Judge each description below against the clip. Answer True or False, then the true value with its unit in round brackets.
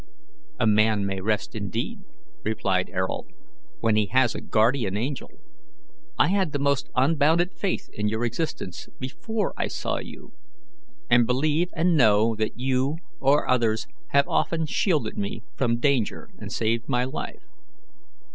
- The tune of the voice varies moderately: True (5.0 semitones)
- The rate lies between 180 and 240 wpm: False (145 wpm)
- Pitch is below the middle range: True (125 Hz)